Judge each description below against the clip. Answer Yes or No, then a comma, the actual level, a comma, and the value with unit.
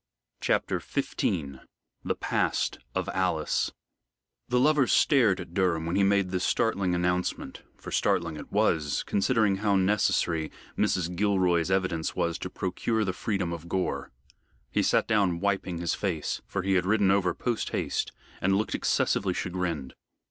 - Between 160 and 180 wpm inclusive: No, average, 150 wpm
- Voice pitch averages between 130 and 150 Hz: No, very low, 95 Hz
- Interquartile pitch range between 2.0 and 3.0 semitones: Yes, average, 2.7 semitones